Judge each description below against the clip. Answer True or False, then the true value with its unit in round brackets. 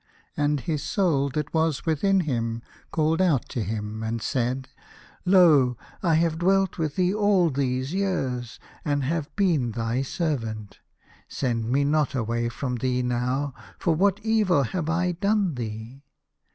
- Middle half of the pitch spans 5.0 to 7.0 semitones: True (5.6 semitones)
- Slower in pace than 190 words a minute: True (155 wpm)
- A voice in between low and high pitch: True (145 Hz)